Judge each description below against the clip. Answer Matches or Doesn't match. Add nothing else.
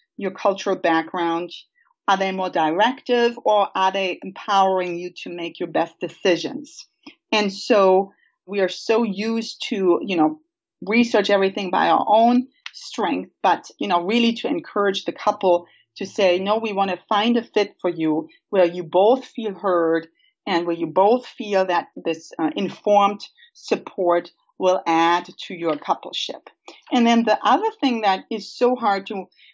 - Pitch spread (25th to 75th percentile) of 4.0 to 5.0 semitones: Matches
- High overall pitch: Matches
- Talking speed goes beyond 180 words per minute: Doesn't match